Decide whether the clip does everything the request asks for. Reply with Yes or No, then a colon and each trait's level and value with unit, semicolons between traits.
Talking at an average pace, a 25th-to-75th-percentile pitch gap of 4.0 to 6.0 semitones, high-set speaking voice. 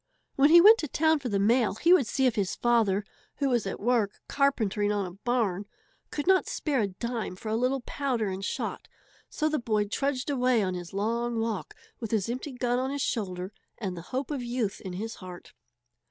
No: fast, 210 wpm; average, 4.6 semitones; high, 235 Hz